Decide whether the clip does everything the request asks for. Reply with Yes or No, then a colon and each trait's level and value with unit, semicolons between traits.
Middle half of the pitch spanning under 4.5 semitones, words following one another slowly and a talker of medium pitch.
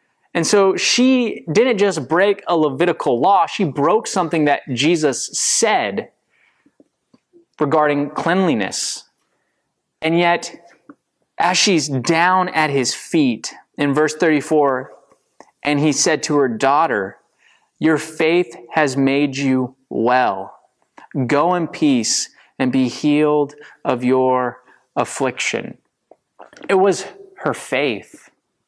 Yes: average, 4.0 semitones; slow, 110 wpm; medium, 155 Hz